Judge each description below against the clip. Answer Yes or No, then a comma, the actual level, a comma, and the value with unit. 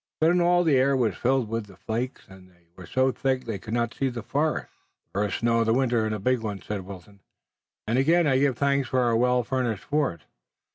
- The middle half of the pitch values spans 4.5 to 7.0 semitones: No, average, 3.8 semitones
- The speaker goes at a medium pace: No, fast, 235 wpm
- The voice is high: No, low, 120 Hz